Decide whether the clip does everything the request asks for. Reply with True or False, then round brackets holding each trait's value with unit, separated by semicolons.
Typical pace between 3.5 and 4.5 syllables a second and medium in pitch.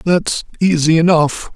True (4.0 syllables/s; 165 Hz)